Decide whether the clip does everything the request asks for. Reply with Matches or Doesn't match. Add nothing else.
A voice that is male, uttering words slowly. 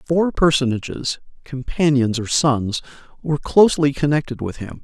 Matches